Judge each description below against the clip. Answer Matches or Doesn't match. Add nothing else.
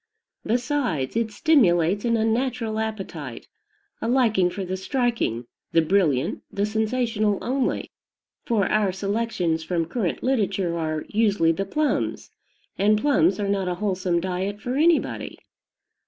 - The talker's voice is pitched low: Doesn't match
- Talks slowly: Matches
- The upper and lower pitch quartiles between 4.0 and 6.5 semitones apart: Matches